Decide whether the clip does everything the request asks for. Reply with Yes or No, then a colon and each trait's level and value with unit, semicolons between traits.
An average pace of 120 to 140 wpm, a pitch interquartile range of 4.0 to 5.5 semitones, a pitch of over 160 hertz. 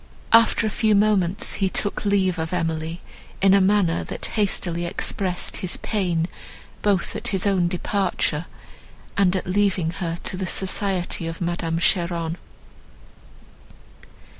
No: slow, 135 wpm; average, 2.7 semitones; medium, 185 Hz